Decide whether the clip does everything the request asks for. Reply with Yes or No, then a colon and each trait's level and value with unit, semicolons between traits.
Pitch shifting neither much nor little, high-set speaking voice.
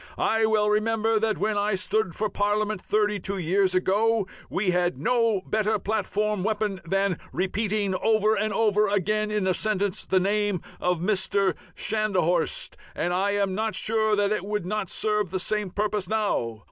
No: narrow, 2.1 semitones; high, 210 Hz